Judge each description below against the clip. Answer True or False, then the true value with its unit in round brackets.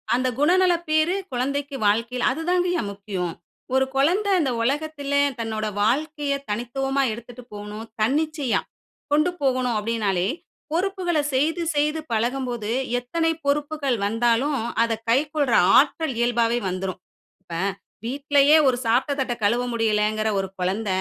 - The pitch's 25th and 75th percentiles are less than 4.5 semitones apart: False (4.8 semitones)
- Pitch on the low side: False (255 Hz)